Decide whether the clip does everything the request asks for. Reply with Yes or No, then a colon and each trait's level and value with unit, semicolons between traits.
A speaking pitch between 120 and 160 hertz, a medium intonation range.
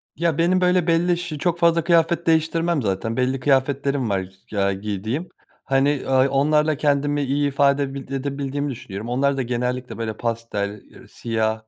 Yes: medium, 140 Hz; average, 4.7 semitones